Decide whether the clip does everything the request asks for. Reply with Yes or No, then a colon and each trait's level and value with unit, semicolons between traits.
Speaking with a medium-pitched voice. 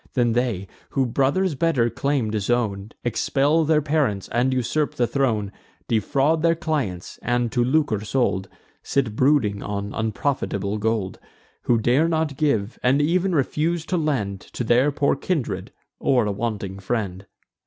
No: low, 125 Hz